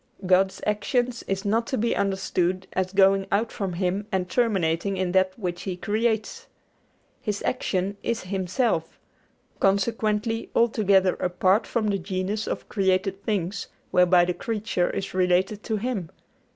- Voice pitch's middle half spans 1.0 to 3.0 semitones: Yes, narrow, 2.6 semitones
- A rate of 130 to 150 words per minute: Yes, average, 140 wpm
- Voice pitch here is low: No, high, 195 Hz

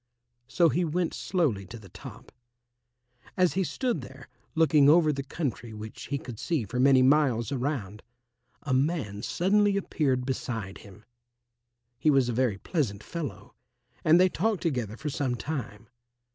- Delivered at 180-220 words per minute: No, average, 155 wpm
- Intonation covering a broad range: Yes, wide, 6.0 semitones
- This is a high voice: No, low, 135 Hz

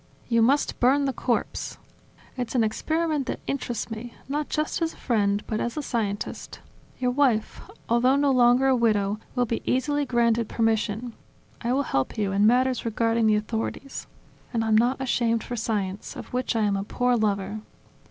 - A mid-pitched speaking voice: No, high, 235 Hz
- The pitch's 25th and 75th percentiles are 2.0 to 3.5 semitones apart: Yes, average, 3.0 semitones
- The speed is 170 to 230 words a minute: Yes, average, 180 wpm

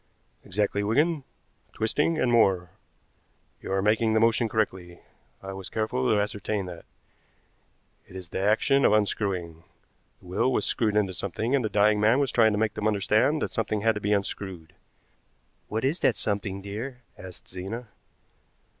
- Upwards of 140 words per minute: Yes, average, 165 wpm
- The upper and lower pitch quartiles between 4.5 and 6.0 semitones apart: No, average, 2.7 semitones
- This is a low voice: Yes, low, 105 Hz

